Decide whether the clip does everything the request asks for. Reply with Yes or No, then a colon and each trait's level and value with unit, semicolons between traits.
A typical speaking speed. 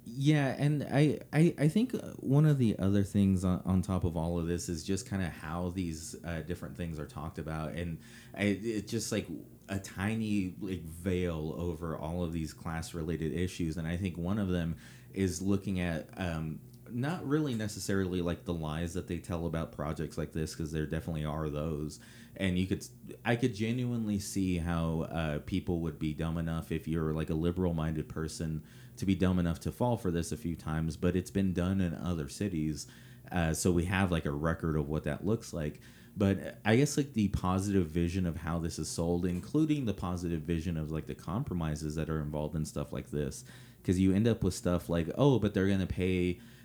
No: fast, 210 wpm